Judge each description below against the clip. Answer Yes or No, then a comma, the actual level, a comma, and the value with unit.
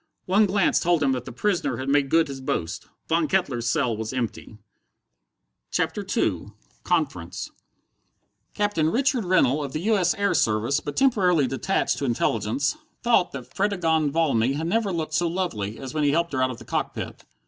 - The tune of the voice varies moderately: No, wide, 5.8 semitones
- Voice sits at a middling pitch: Yes, medium, 155 Hz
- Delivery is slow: No, average, 180 wpm